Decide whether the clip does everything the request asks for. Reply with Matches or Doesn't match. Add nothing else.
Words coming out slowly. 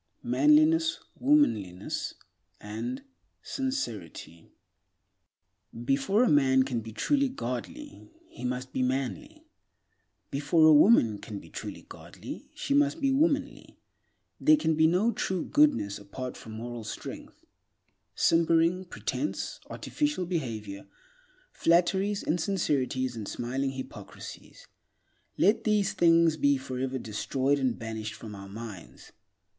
Matches